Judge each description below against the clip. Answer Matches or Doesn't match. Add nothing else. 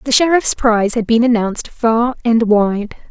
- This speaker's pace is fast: Doesn't match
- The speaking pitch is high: Matches